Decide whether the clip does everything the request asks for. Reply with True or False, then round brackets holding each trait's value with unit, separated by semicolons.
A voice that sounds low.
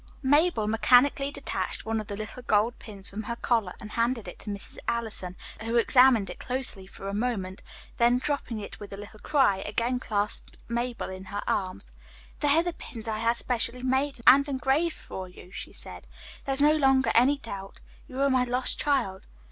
False (235 Hz)